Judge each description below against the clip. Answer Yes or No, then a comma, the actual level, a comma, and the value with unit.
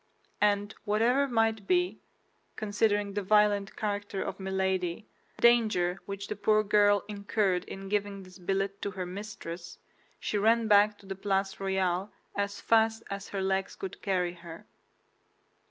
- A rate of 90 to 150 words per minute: Yes, average, 140 wpm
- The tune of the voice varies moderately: No, narrow, 1.7 semitones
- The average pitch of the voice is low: No, high, 200 Hz